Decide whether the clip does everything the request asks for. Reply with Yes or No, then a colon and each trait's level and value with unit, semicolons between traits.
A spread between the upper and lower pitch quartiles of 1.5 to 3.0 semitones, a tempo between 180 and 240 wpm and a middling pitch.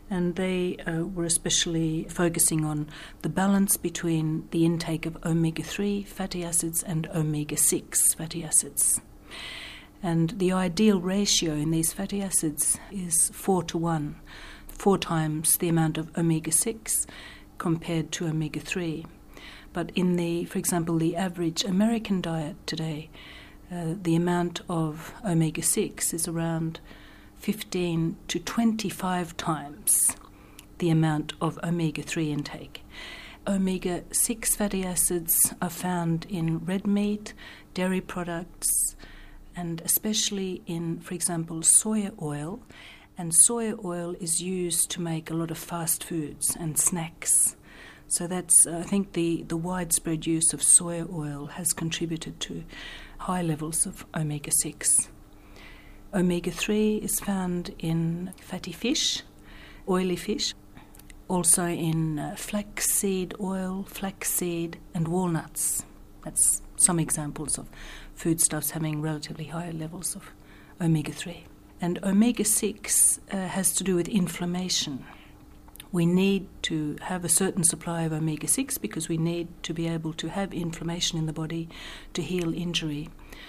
No: narrow, 2.4 semitones; slow, 135 wpm; medium, 170 Hz